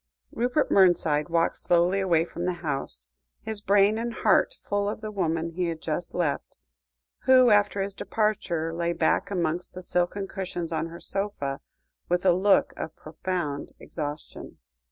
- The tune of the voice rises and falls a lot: No, average, 3.5 semitones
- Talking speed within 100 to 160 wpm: Yes, average, 155 wpm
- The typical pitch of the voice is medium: Yes, medium, 175 Hz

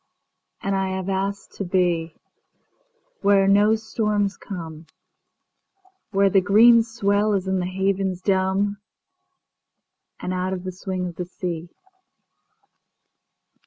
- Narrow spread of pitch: Yes, narrow, 2.2 semitones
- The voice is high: Yes, high, 195 Hz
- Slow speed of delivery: Yes, slow, 105 wpm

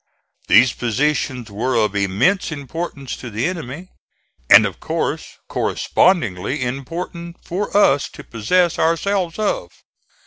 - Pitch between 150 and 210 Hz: No, medium, 140 Hz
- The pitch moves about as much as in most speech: No, wide, 6.6 semitones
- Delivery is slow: Yes, slow, 115 wpm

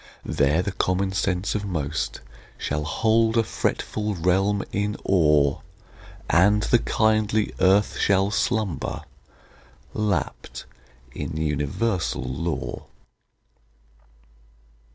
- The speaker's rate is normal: No, slow, 90 wpm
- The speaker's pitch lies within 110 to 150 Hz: No, very low, 95 Hz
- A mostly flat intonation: No, average, 5.0 semitones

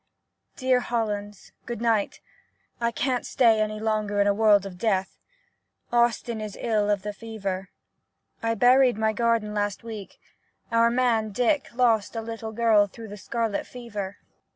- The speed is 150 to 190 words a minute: Yes, average, 155 wpm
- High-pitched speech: Yes, high, 220 Hz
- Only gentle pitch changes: Yes, narrow, 2.3 semitones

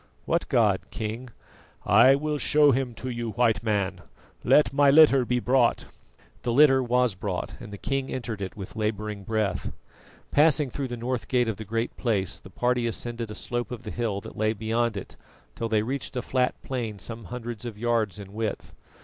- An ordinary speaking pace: Yes, average, 190 wpm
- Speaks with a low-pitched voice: Yes, low, 120 Hz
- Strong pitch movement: No, average, 2.9 semitones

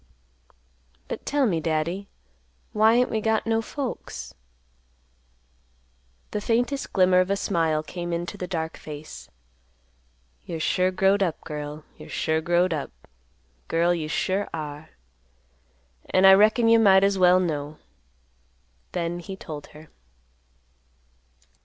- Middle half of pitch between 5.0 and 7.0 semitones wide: No, average, 4.1 semitones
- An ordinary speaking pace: No, slow, 130 wpm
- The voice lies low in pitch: No, medium, 180 Hz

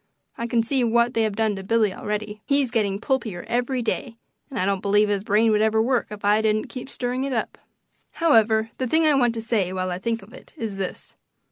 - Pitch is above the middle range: Yes, high, 225 Hz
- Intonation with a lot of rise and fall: No, average, 2.8 semitones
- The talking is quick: Yes, fast, 235 wpm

